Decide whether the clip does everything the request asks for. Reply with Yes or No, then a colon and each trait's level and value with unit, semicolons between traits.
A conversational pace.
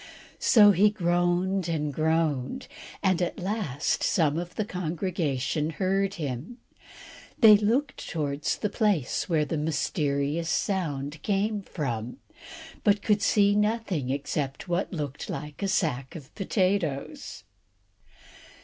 No: slow, 120 wpm